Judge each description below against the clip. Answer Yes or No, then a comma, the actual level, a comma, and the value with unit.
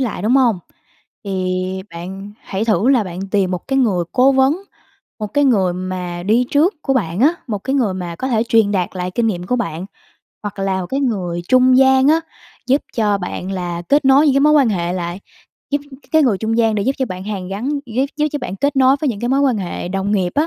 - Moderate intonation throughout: No, wide, 6.2 semitones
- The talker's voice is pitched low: No, high, 215 Hz